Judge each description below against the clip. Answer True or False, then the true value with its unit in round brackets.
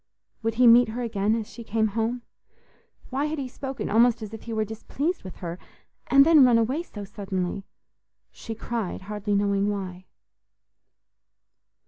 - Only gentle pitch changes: False (3.4 semitones)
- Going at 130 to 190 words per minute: True (160 wpm)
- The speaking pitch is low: False (225 Hz)